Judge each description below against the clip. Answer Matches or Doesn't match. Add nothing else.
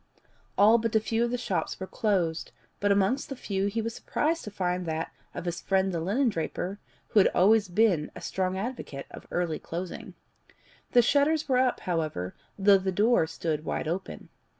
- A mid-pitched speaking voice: Doesn't match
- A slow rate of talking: Doesn't match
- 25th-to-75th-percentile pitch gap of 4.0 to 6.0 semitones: Matches